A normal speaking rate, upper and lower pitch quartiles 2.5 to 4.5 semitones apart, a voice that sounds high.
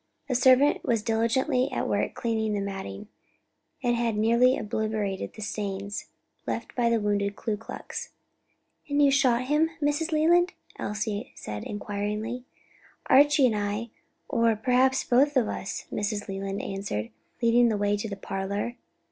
Yes: average, 150 wpm; average, 3.8 semitones; high, 225 Hz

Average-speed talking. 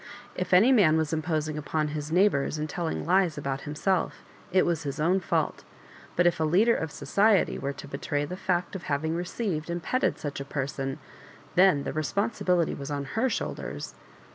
Yes: average, 185 wpm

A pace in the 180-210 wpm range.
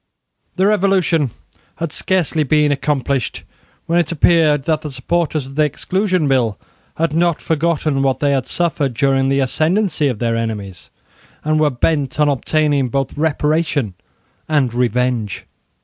No: average, 145 wpm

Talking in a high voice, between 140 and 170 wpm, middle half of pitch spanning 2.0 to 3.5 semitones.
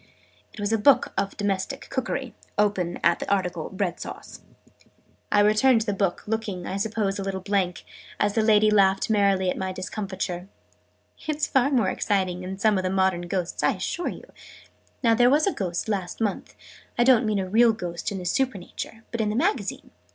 No: high, 200 Hz; average, 190 wpm; average, 3.0 semitones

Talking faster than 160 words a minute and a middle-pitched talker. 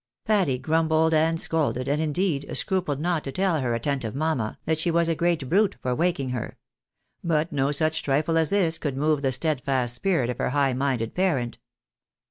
Yes: average, 185 wpm; medium, 155 Hz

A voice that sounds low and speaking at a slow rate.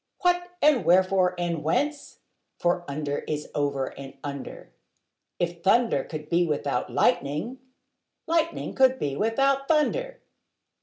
No: medium, 180 Hz; slow, 120 wpm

